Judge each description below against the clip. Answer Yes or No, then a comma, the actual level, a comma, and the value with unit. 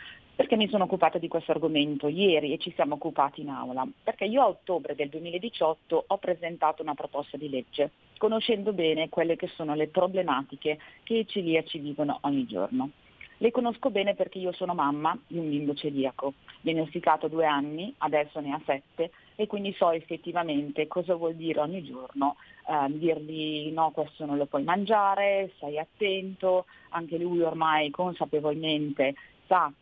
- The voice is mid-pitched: Yes, medium, 160 Hz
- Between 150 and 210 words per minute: Yes, average, 165 wpm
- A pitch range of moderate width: Yes, average, 3.7 semitones